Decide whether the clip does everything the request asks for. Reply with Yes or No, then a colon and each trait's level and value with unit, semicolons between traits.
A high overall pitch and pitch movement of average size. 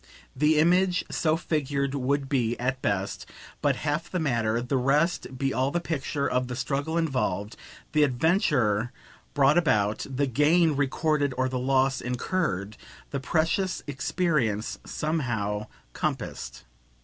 No: low, 135 Hz; average, 4.0 semitones